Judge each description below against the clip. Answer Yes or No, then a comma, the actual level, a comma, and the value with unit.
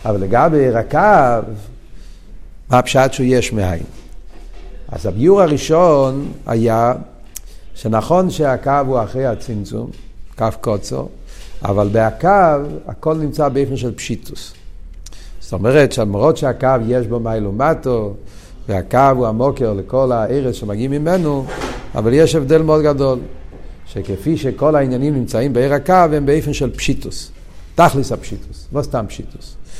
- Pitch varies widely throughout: No, average, 4.9 semitones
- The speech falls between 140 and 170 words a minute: No, average, 125 wpm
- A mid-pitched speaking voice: No, low, 125 Hz